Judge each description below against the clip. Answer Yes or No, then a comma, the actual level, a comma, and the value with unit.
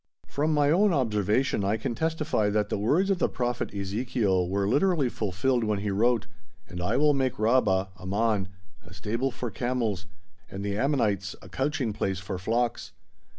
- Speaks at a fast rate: No, average, 170 wpm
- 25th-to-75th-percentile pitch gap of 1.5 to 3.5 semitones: No, average, 5.0 semitones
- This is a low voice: Yes, low, 110 Hz